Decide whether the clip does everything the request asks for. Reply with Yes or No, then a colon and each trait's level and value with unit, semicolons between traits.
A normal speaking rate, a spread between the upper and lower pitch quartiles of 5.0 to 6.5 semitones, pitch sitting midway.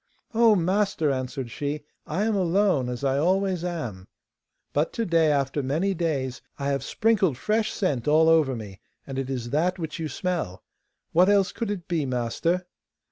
Yes: average, 175 wpm; wide, 5.6 semitones; medium, 160 Hz